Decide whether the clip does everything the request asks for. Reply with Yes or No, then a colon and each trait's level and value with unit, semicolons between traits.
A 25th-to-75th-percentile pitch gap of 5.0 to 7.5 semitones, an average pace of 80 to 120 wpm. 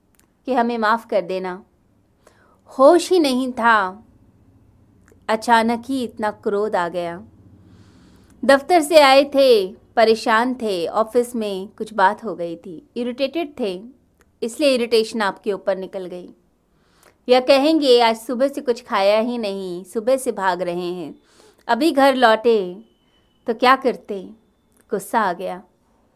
No: average, 5.3 semitones; average, 135 wpm